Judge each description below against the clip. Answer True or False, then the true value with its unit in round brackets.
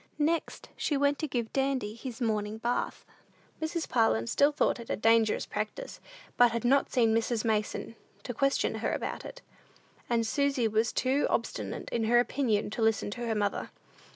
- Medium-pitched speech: False (235 Hz)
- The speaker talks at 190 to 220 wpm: False (175 wpm)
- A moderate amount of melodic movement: True (3.8 semitones)